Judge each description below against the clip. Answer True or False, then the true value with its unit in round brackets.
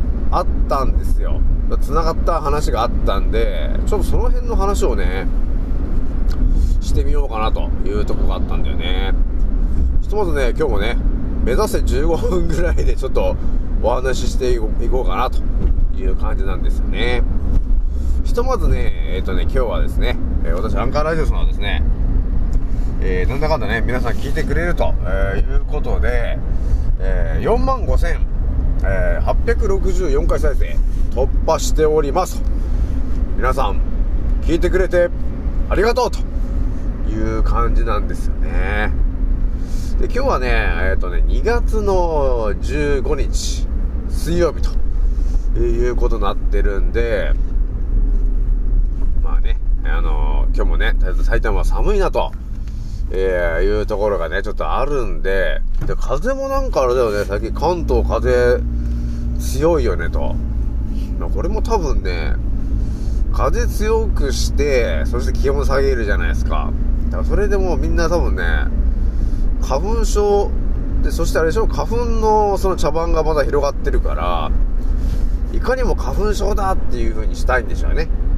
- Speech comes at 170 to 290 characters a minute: True (270 characters per minute)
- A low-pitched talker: True (85 Hz)